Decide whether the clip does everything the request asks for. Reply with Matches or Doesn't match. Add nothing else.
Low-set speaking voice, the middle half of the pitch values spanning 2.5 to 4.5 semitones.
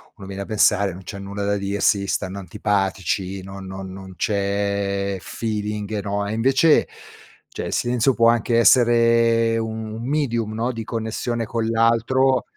Matches